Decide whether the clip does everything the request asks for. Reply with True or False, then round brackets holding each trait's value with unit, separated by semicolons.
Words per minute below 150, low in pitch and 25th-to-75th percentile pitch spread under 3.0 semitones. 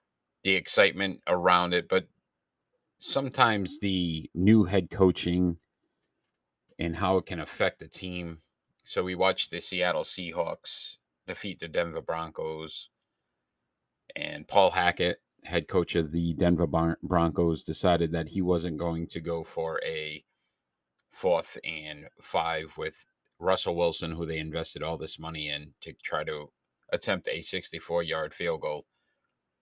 True (140 wpm; 85 Hz; 2.6 semitones)